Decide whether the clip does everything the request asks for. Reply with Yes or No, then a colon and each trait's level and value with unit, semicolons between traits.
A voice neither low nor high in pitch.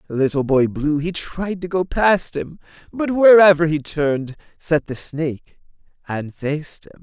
Yes: medium, 160 Hz